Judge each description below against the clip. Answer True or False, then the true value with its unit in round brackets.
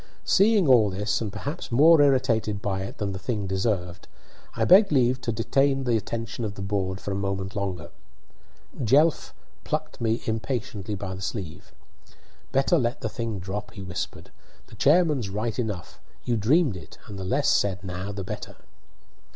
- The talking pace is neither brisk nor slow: True (170 wpm)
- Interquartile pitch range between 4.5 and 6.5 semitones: True (5.0 semitones)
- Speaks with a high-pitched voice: False (105 Hz)